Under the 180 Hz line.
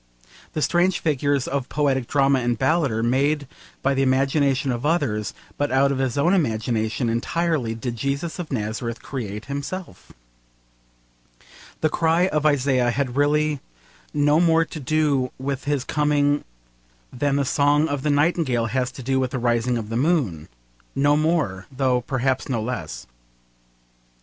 Yes: low, 135 Hz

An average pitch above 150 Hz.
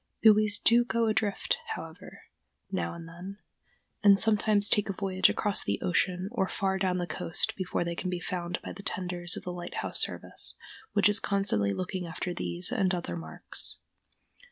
Yes: medium, 185 Hz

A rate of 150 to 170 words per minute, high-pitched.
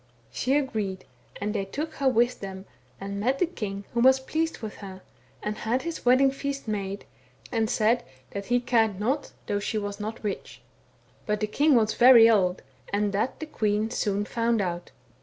No: average, 185 wpm; high, 220 Hz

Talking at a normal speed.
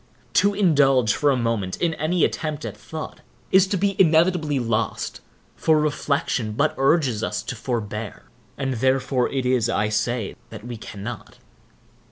Yes: average, 155 wpm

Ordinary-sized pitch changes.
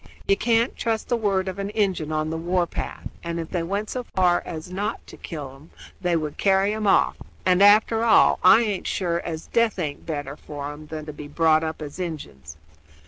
Yes: average, 4.5 semitones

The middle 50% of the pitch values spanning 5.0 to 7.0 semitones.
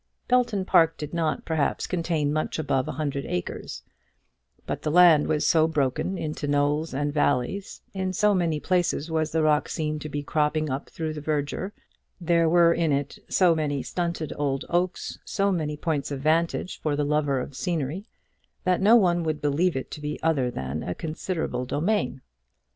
No: average, 2.9 semitones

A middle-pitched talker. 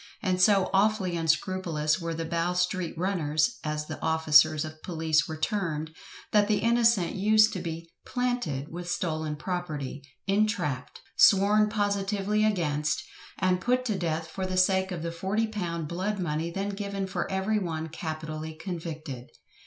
Yes: medium, 175 Hz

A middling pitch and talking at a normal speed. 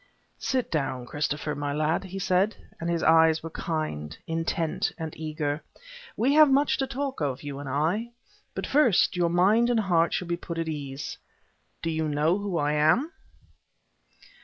Yes: medium, 165 Hz; average, 170 wpm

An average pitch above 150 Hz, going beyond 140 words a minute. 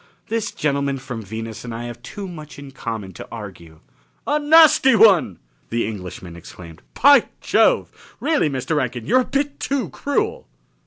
No: low, 135 Hz; average, 160 wpm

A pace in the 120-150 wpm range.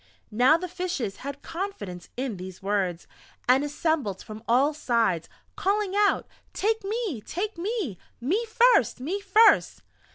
Yes: slow, 135 wpm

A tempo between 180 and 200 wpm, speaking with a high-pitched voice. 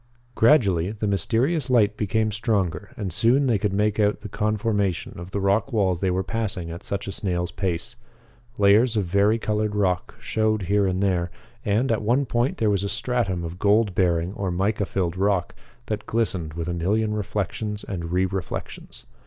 No: average, 185 wpm; low, 100 Hz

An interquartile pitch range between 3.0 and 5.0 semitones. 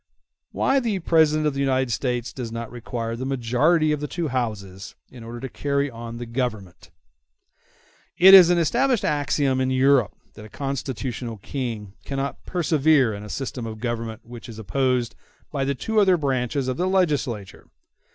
Yes: average, 4.3 semitones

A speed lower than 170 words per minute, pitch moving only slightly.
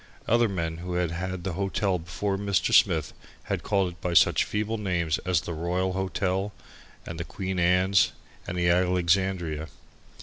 Yes: average, 160 wpm; narrow, 1.9 semitones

